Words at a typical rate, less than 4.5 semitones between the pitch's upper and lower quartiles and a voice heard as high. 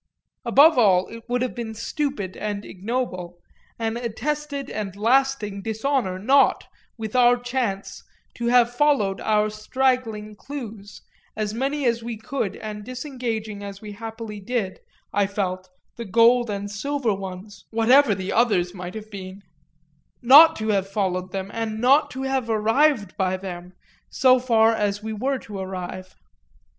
Yes: average, 150 wpm; average, 3.8 semitones; high, 220 Hz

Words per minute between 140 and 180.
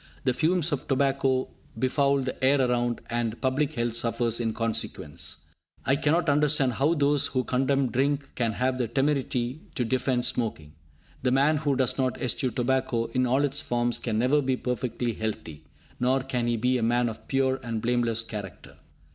Yes: average, 175 wpm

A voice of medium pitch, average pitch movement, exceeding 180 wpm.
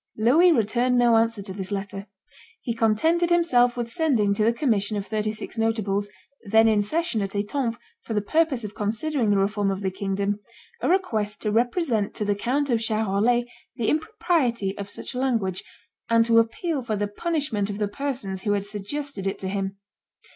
No: high, 220 Hz; average, 3.5 semitones; average, 190 wpm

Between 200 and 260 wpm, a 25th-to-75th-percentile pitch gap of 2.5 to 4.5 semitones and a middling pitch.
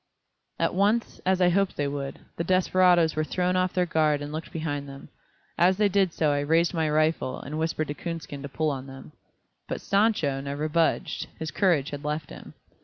Yes: fast, 205 wpm; average, 3.8 semitones; medium, 160 Hz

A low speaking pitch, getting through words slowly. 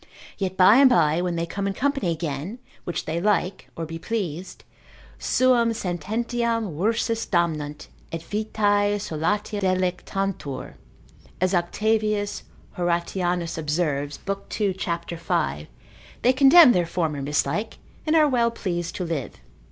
No: medium, 185 Hz; slow, 130 wpm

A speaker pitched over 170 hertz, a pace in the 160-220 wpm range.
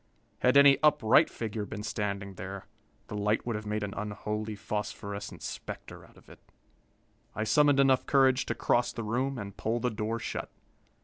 No: low, 110 Hz; average, 175 wpm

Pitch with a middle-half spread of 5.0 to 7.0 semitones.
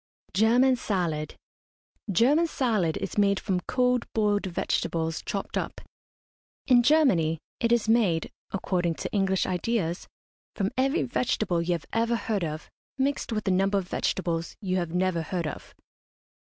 Yes: average, 5.3 semitones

